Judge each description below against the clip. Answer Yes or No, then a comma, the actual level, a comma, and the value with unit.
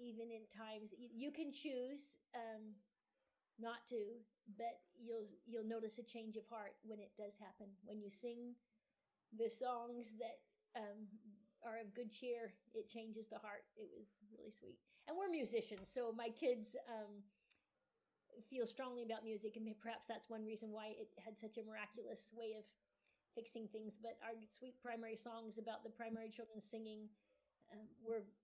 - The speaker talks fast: No, average, 165 wpm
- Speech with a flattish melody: Yes, narrow, 1.6 semitones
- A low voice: No, high, 225 Hz